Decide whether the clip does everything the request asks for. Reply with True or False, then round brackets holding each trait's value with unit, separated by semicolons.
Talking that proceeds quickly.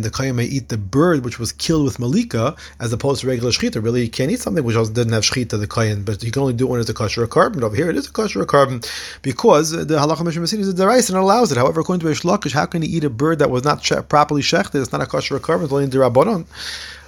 True (295 wpm)